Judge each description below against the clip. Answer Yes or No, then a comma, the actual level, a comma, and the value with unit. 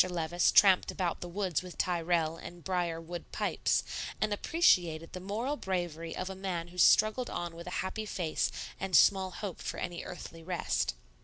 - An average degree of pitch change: No, narrow, 2.2 semitones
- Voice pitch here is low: No, medium, 180 Hz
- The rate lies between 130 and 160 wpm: No, average, 175 wpm